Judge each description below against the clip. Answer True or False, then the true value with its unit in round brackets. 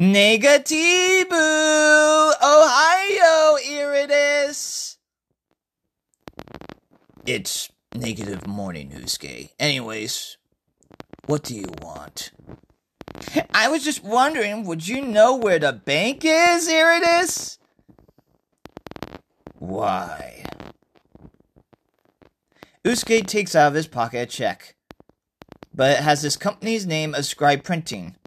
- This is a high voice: True (225 Hz)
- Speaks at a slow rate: True (90 wpm)